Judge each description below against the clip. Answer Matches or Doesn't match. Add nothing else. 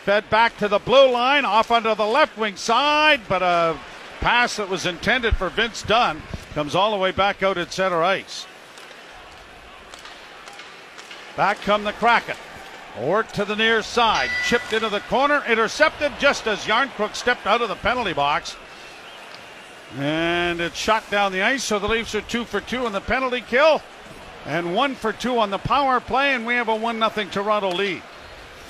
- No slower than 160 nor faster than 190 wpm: Matches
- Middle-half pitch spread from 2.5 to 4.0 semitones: Matches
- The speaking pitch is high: Matches